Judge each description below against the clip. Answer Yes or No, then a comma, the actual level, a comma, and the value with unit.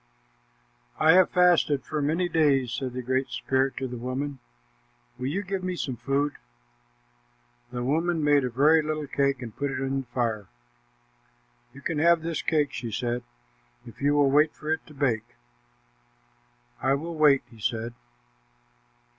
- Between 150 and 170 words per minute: Yes, average, 165 wpm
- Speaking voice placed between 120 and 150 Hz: Yes, medium, 140 Hz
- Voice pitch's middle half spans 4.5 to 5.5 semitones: No, average, 3.4 semitones